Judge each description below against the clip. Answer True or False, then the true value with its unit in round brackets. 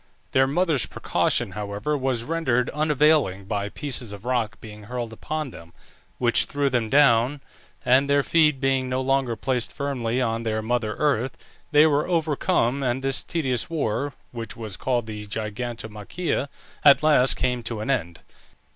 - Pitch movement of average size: True (4.1 semitones)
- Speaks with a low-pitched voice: True (125 Hz)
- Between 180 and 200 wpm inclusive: False (155 wpm)